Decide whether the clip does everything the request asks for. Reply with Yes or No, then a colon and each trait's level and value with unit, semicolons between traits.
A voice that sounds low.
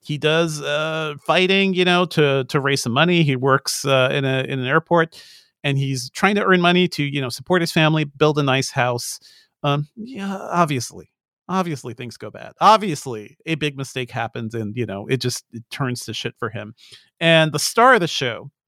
No: medium, 145 Hz